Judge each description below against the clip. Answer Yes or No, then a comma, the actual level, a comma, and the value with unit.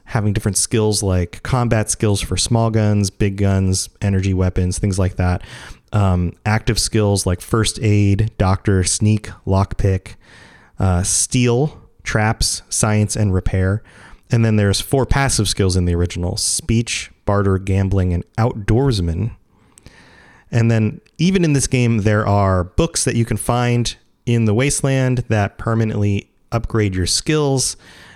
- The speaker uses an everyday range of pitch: Yes, average, 3.1 semitones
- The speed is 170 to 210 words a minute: No, average, 140 wpm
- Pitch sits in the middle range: No, low, 105 Hz